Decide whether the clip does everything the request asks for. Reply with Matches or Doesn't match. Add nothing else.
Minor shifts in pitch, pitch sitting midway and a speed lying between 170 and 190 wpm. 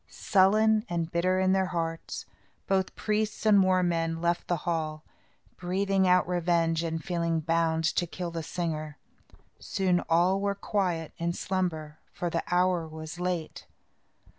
Doesn't match